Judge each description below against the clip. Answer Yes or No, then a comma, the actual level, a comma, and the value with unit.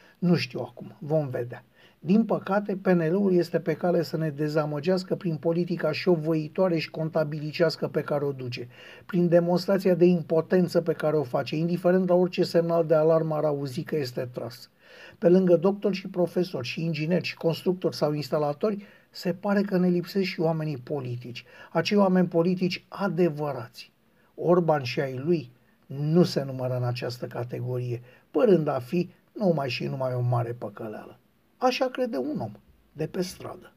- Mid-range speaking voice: Yes, medium, 165 Hz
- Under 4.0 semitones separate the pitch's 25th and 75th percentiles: Yes, average, 3.3 semitones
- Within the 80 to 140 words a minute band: No, average, 165 wpm